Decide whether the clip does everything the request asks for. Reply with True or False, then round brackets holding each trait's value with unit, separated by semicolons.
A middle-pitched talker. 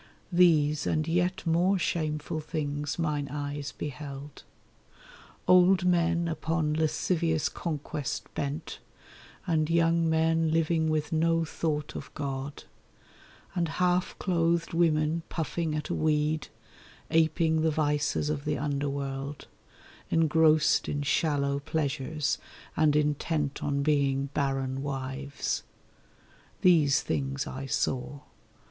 True (155 Hz)